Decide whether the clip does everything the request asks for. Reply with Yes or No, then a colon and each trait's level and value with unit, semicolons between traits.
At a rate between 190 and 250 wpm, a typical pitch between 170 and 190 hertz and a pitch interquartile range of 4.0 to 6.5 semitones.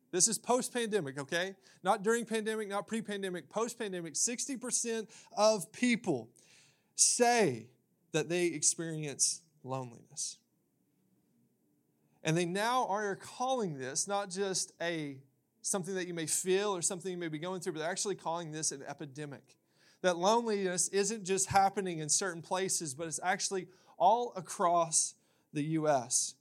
No: average, 140 wpm; medium, 185 Hz; average, 4.5 semitones